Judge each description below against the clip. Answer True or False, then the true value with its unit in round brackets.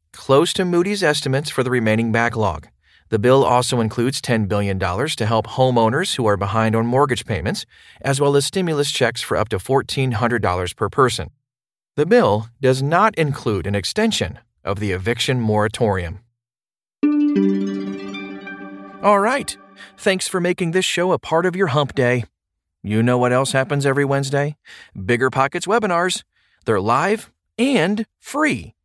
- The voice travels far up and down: True (6.3 semitones)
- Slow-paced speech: False (150 wpm)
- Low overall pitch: True (125 Hz)